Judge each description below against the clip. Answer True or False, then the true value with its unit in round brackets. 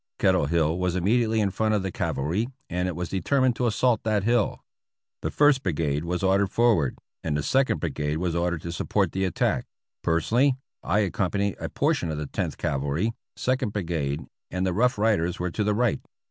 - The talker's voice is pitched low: True (95 Hz)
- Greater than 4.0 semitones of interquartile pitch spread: True (4.9 semitones)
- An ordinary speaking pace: True (190 wpm)